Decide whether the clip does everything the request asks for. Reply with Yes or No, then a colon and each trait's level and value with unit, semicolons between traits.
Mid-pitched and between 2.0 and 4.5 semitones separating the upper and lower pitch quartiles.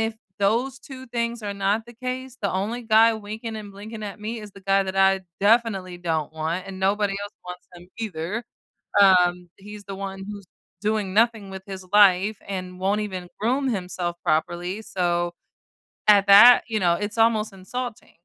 No: high, 200 Hz; average, 2.9 semitones